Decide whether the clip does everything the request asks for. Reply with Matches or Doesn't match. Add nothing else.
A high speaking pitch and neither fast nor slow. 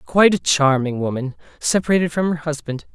Doesn't match